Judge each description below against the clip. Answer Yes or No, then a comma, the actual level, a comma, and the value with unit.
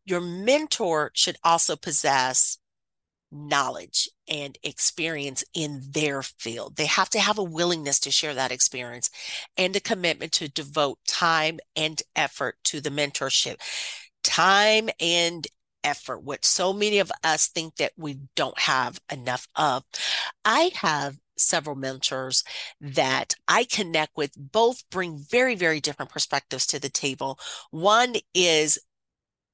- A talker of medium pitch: Yes, medium, 155 Hz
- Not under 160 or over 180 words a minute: No, slow, 135 wpm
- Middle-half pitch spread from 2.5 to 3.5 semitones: No, average, 4.2 semitones